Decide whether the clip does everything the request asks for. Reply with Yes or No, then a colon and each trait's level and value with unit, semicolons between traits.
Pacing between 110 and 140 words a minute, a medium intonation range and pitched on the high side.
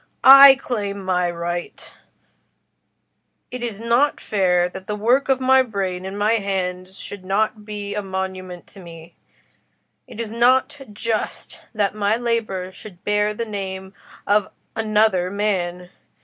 Yes: slow, 135 wpm; average, 3.3 semitones; high, 205 Hz